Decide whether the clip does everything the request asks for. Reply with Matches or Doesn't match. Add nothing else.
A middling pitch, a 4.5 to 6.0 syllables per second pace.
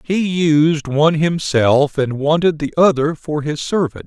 Doesn't match